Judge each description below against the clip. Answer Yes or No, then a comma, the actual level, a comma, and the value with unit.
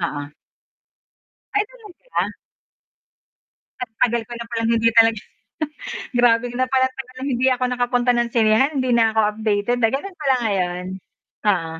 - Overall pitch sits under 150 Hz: No, high, 235 Hz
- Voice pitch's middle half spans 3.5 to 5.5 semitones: No, average, 2.7 semitones